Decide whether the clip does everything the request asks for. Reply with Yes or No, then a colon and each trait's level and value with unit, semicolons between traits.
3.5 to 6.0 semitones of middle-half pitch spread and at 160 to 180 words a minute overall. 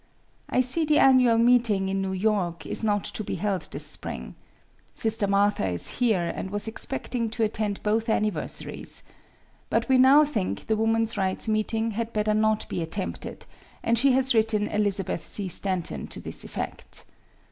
No: average, 2.7 semitones; average, 170 wpm